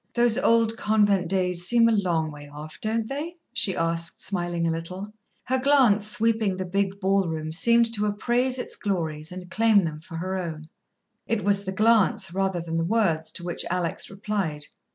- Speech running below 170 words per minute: No, average, 180 wpm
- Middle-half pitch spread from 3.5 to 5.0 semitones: Yes, average, 4.6 semitones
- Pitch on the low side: No, high, 190 Hz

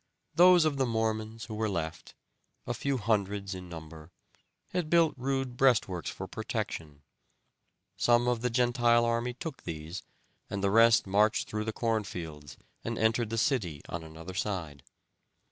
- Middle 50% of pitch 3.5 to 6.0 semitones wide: Yes, average, 5.2 semitones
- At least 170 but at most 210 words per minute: No, average, 155 wpm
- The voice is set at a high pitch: No, low, 110 Hz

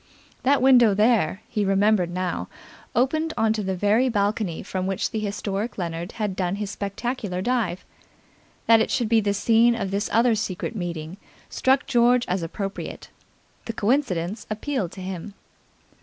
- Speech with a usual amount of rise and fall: Yes, average, 3.8 semitones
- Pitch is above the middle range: Yes, high, 210 Hz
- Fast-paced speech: No, average, 155 wpm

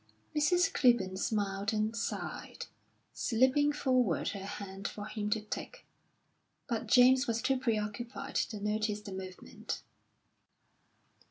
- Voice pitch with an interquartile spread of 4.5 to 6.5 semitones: No, average, 3.9 semitones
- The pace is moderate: No, slow, 115 wpm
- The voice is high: Yes, high, 220 Hz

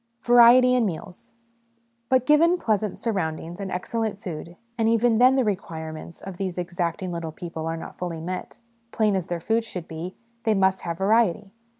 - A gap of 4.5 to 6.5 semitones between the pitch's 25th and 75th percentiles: Yes, average, 4.9 semitones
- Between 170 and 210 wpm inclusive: Yes, average, 180 wpm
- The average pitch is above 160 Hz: Yes, high, 190 Hz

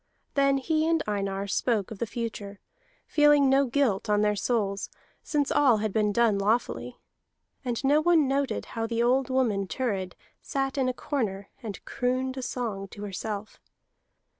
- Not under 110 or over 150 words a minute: No, average, 165 wpm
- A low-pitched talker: No, high, 235 Hz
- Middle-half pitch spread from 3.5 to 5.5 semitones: Yes, average, 4.7 semitones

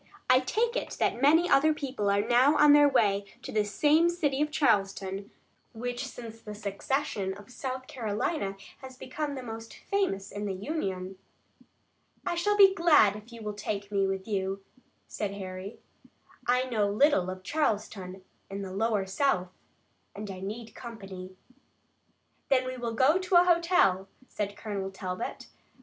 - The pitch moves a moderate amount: No, wide, 6.1 semitones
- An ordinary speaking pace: Yes, average, 160 wpm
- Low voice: No, high, 220 Hz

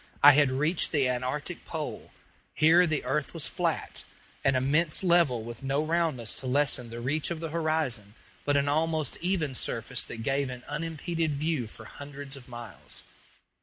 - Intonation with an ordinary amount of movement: Yes, average, 3.8 semitones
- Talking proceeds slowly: No, average, 165 wpm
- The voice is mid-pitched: Yes, medium, 145 Hz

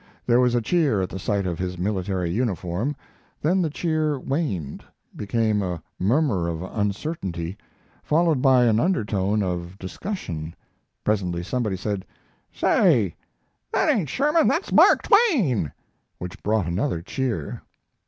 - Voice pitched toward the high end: No, low, 105 Hz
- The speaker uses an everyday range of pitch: No, wide, 7.8 semitones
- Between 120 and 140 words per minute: Yes, slow, 135 wpm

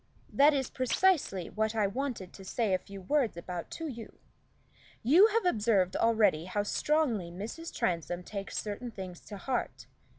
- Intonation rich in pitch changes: Yes, wide, 6.2 semitones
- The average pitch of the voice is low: No, high, 215 Hz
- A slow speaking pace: No, average, 160 wpm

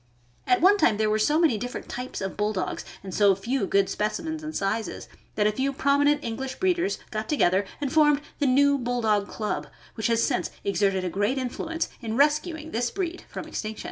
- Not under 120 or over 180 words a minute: No, fast, 205 wpm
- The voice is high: Yes, high, 245 Hz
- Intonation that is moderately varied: No, wide, 5.9 semitones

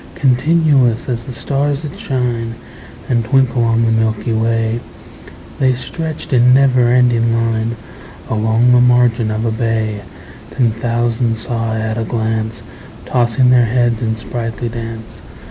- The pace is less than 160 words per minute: Yes, average, 145 wpm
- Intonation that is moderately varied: No, narrow, 1.8 semitones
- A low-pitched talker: Yes, low, 115 Hz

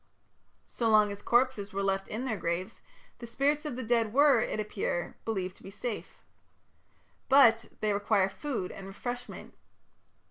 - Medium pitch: No, high, 220 Hz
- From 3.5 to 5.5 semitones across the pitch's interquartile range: Yes, average, 3.8 semitones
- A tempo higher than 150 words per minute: Yes, average, 165 wpm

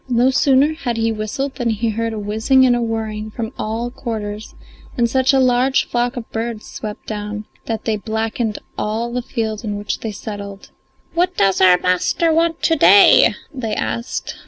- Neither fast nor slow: Yes, average, 185 wpm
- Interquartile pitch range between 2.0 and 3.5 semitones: Yes, average, 2.7 semitones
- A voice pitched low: No, high, 225 Hz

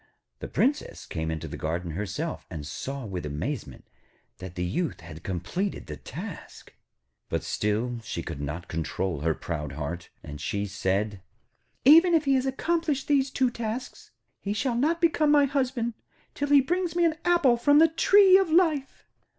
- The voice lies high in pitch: Yes, high, 215 Hz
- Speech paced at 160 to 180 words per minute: Yes, average, 170 wpm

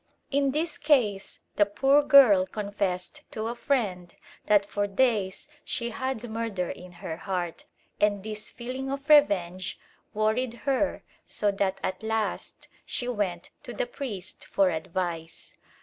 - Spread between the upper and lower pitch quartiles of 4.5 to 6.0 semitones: Yes, wide, 5.4 semitones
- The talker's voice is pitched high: Yes, high, 210 Hz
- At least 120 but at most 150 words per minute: Yes, average, 140 wpm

